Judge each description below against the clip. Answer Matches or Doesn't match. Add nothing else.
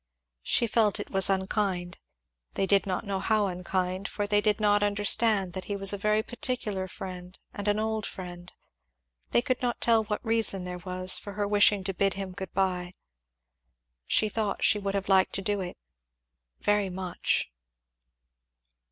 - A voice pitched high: Matches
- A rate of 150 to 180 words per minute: Matches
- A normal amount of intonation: Doesn't match